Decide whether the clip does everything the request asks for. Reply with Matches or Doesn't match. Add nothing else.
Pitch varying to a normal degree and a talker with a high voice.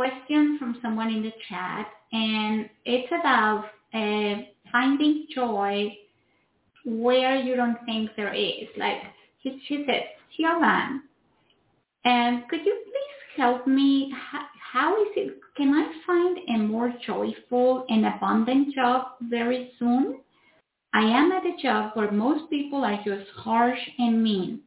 Matches